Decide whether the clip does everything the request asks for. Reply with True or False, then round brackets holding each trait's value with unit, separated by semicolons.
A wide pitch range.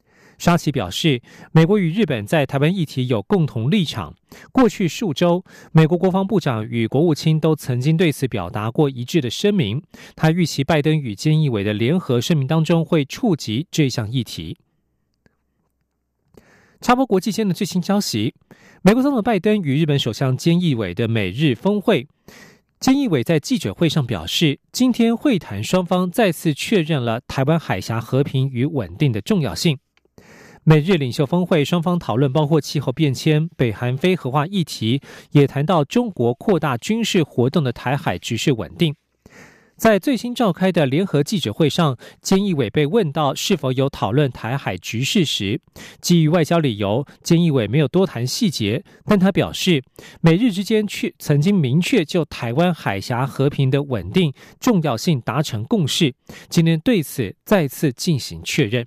True (5.7 semitones)